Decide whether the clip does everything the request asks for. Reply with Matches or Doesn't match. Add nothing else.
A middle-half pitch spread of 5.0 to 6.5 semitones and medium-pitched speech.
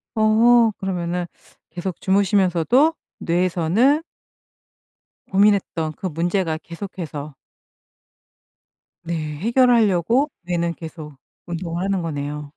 Doesn't match